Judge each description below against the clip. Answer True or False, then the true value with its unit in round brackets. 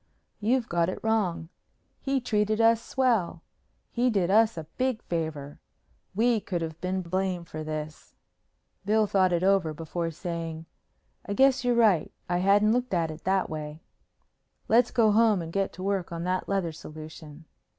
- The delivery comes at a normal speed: True (165 wpm)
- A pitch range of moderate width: True (4.8 semitones)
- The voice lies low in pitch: False (185 Hz)